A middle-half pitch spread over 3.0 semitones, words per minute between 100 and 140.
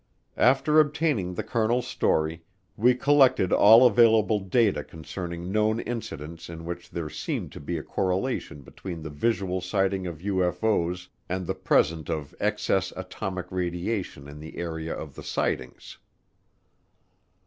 Yes: average, 4.8 semitones; slow, 135 wpm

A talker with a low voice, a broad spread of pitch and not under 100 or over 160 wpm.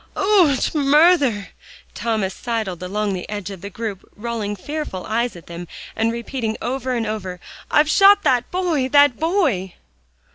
No: high, 235 Hz; wide, 6.1 semitones; average, 150 wpm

